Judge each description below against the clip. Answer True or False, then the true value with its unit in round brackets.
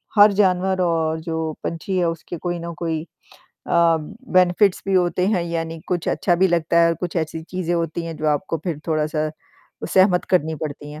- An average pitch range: False (2.1 semitones)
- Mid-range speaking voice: True (170 Hz)